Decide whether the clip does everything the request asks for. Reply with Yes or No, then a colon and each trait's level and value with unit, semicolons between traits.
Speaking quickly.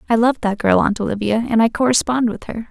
Yes: fast, 245 wpm